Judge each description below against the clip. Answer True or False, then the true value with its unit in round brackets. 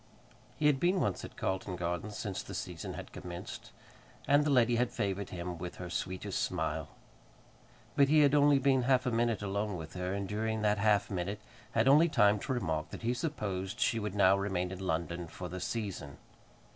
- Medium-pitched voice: False (100 Hz)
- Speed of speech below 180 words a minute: False (195 wpm)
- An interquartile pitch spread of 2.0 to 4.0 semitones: False (5.1 semitones)